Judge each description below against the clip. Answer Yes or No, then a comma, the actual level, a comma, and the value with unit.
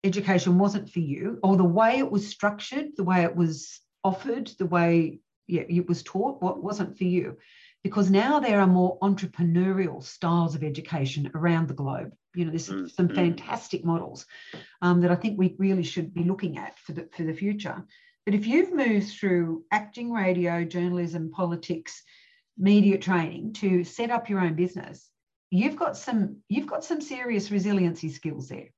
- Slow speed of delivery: No, average, 175 wpm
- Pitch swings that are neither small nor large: Yes, average, 3.3 semitones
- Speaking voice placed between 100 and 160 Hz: No, medium, 185 Hz